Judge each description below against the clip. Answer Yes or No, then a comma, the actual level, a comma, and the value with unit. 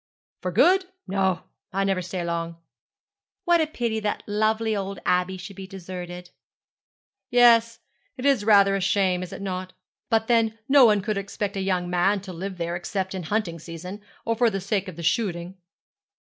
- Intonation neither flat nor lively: Yes, average, 3.3 semitones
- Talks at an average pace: Yes, average, 185 wpm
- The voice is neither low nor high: No, high, 195 Hz